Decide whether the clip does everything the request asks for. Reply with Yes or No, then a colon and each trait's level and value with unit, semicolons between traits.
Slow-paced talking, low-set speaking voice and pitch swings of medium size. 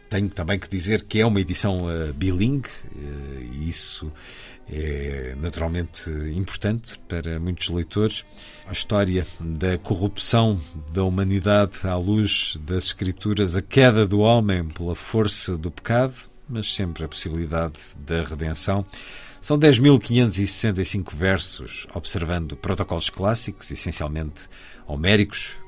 Yes: slow, 115 wpm; very low, 95 Hz; average, 3.9 semitones